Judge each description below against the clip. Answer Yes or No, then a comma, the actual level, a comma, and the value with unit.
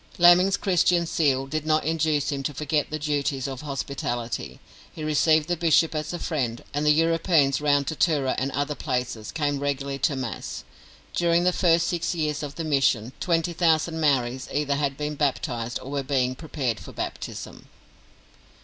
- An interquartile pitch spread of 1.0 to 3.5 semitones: Yes, average, 3.0 semitones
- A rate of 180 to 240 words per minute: No, average, 170 wpm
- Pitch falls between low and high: Yes, medium, 150 Hz